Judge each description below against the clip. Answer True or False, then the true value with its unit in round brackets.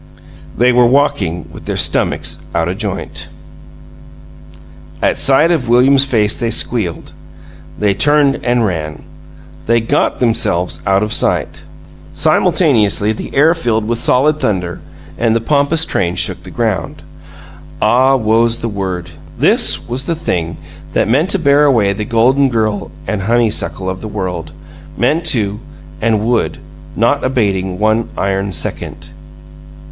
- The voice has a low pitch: True (115 Hz)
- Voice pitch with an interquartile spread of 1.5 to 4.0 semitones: False (4.8 semitones)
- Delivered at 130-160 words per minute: True (140 wpm)